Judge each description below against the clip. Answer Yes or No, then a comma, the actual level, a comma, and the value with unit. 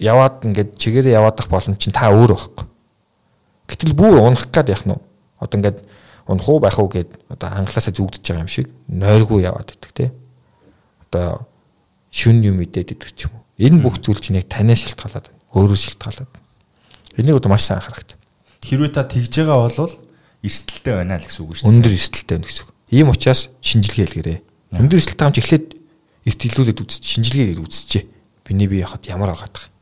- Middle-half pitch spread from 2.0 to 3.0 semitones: No, average, 4.6 semitones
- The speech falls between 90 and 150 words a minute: No, average, 185 wpm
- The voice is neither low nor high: No, low, 110 Hz